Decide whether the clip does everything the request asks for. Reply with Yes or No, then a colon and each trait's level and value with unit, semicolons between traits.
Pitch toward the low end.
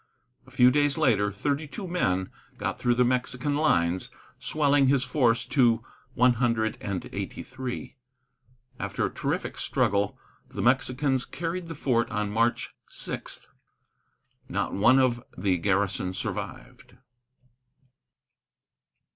Yes: low, 125 Hz